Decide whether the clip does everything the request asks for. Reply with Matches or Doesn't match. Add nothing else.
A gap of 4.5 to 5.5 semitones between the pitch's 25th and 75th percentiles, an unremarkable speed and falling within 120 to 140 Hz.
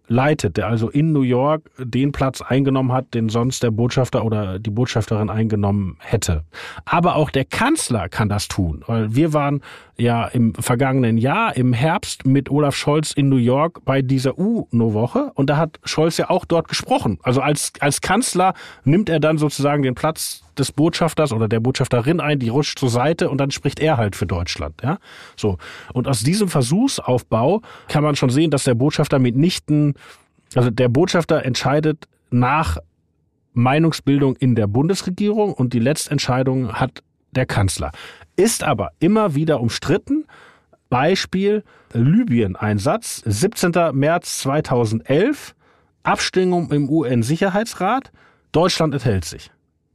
Matches